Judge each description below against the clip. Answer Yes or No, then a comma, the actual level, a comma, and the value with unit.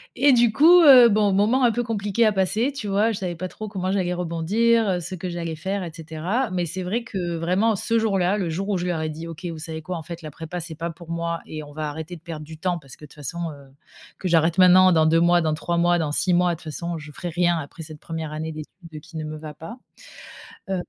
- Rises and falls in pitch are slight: No, average, 3.5 semitones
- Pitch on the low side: No, medium, 175 Hz